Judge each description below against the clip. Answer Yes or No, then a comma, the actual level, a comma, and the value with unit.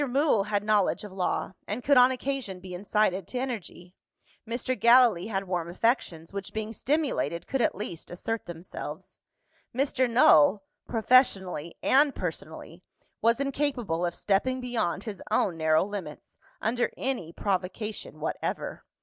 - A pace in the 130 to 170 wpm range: Yes, average, 140 wpm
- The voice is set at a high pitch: Yes, high, 210 Hz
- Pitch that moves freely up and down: Yes, wide, 5.7 semitones